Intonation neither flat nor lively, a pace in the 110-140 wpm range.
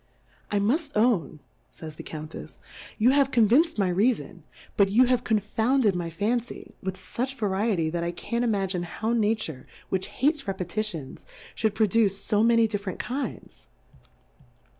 No: average, 4.1 semitones; average, 150 wpm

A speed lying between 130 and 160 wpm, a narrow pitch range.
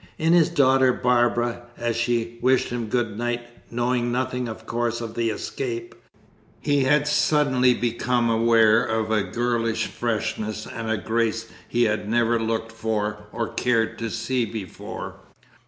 Yes: average, 145 wpm; narrow, 1.8 semitones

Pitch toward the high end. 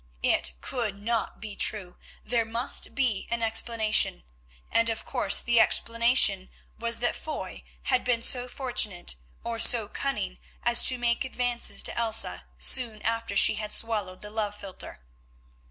Yes: high, 230 Hz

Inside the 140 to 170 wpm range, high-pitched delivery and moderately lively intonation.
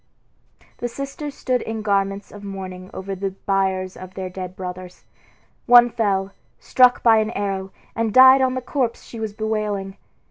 Yes: average, 165 wpm; high, 205 Hz; average, 3.7 semitones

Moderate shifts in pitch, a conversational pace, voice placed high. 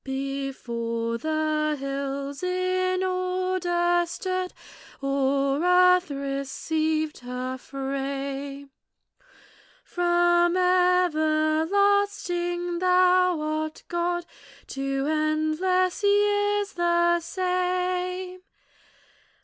No: average, 4.6 semitones; slow, 65 wpm; very high, 345 Hz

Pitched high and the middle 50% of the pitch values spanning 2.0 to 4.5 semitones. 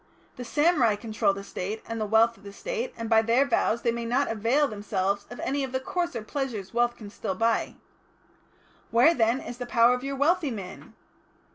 Yes: high, 235 Hz; average, 3.7 semitones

